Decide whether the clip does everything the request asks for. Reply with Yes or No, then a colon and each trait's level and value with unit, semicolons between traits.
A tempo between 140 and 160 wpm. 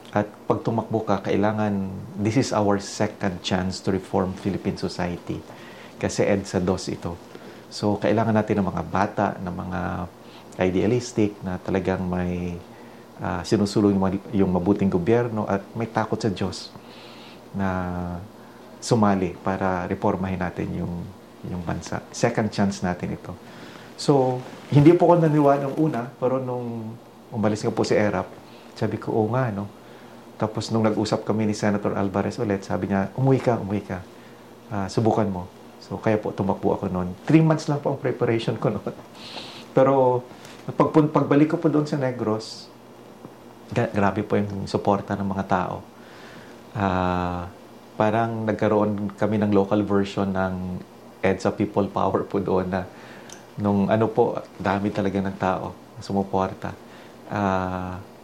Yes: average, 150 wpm